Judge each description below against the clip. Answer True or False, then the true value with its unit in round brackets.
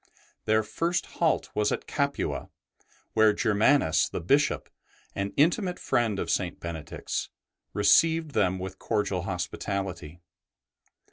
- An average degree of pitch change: False (7.3 semitones)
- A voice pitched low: True (105 Hz)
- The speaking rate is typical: False (115 wpm)